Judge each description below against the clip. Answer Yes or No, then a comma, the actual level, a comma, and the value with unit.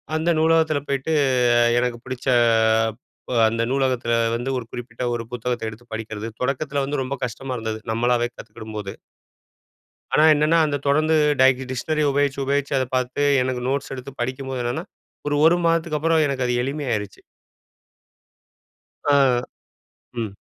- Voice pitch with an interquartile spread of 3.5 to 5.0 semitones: No, average, 3.1 semitones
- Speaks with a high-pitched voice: No, low, 130 Hz